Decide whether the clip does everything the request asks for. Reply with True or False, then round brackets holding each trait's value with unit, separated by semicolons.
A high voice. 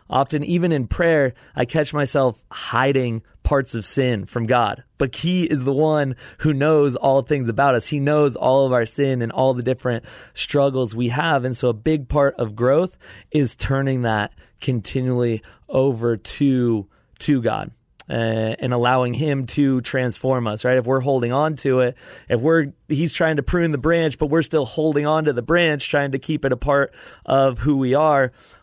False (135 Hz)